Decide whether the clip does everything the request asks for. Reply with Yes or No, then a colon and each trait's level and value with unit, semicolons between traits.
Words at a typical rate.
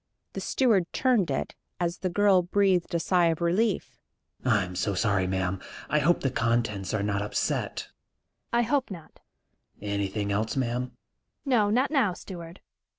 Yes: average, 155 wpm